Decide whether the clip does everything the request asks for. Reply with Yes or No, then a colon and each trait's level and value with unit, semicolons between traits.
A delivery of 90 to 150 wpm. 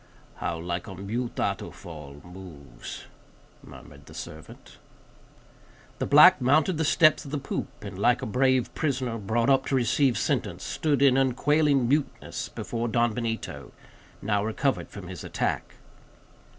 Yes: average, 140 wpm